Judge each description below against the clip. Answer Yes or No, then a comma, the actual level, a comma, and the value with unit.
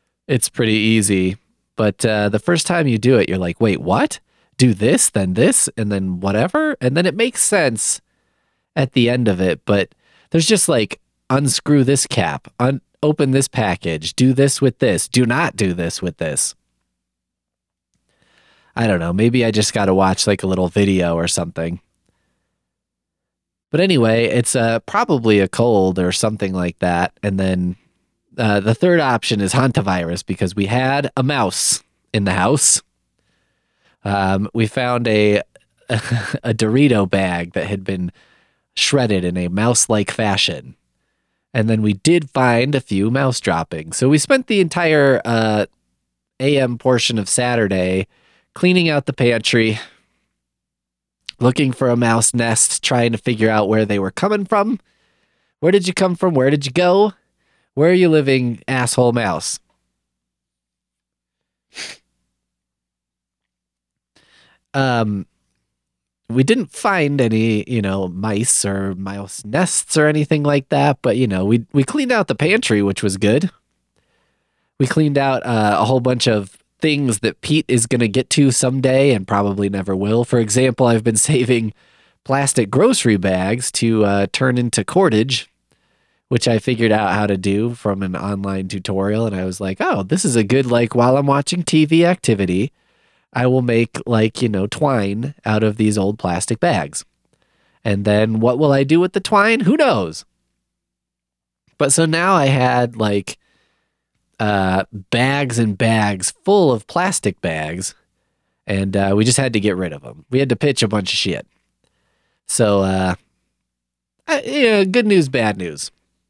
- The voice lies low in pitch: Yes, low, 110 Hz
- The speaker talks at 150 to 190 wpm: Yes, average, 165 wpm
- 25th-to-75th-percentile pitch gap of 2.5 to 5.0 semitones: No, wide, 5.6 semitones